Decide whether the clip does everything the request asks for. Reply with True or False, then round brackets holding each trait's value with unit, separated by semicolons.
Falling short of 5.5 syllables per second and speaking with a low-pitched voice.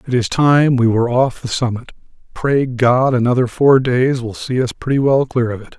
True (5.0 syllables/s; 125 Hz)